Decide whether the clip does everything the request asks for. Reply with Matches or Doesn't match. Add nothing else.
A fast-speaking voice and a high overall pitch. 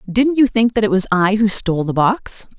Matches